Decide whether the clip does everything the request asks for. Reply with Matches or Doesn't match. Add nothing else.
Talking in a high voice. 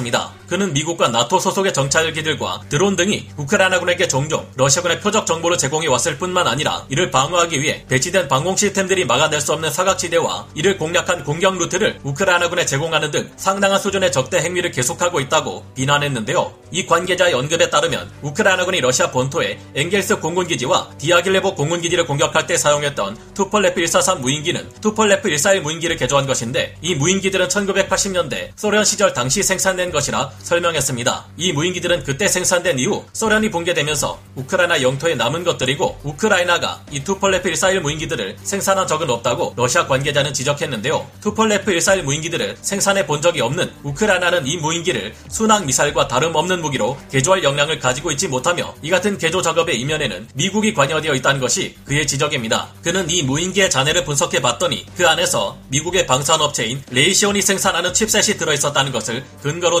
Doesn't match